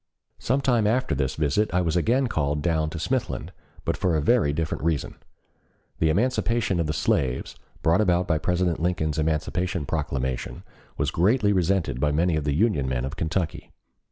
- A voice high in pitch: No, very low, 85 Hz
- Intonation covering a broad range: No, average, 4.5 semitones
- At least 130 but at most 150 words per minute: No, average, 175 wpm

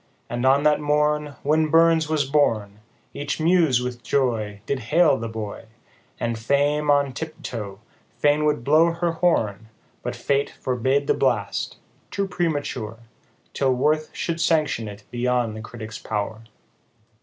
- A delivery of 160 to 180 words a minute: No, average, 150 wpm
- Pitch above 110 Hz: Yes, medium, 140 Hz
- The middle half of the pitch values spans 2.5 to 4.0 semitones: No, average, 4.9 semitones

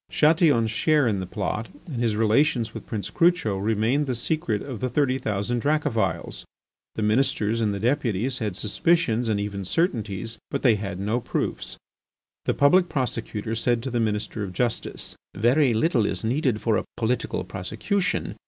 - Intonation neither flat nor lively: Yes, average, 4.4 semitones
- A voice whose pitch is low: Yes, low, 115 Hz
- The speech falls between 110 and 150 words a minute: No, average, 165 wpm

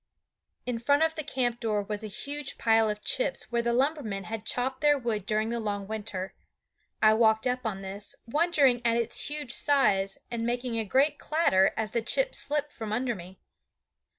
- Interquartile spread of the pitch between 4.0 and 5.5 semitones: Yes, average, 4.5 semitones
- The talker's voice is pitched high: Yes, high, 235 Hz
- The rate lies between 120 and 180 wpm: No, average, 190 wpm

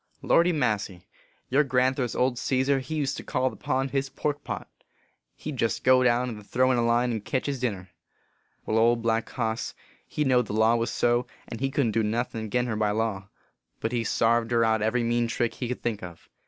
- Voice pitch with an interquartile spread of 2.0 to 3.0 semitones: Yes, narrow, 2.5 semitones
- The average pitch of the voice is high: No, low, 120 Hz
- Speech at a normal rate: No, fast, 235 wpm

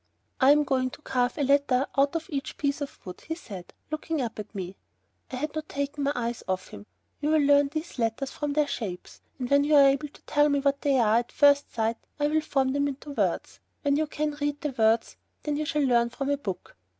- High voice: Yes, very high, 280 Hz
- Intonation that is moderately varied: Yes, average, 3.1 semitones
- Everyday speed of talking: No, fast, 240 wpm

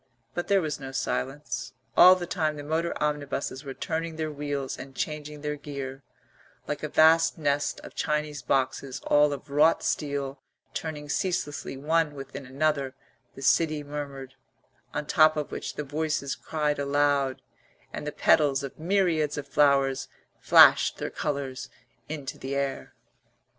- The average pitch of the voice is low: No, medium, 145 Hz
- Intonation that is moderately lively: No, narrow, 2.0 semitones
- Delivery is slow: No, average, 155 wpm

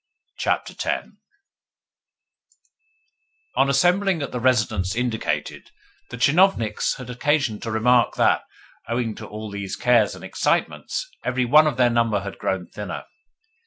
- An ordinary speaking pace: No, slow, 130 wpm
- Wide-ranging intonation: No, average, 3.9 semitones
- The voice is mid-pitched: No, low, 120 Hz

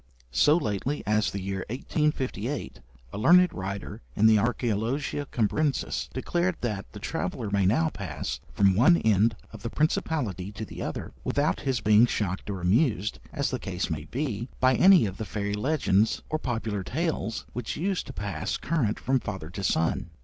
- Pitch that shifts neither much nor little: No, wide, 6.0 semitones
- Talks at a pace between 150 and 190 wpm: Yes, average, 170 wpm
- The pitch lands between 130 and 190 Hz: No, low, 110 Hz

